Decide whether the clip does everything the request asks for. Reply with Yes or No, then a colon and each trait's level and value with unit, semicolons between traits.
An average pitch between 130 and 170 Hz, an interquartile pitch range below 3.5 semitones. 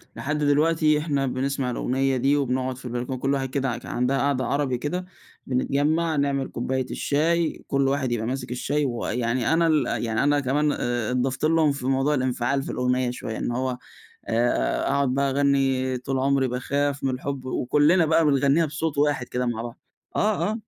Yes: low, 135 Hz; narrow, 2.5 semitones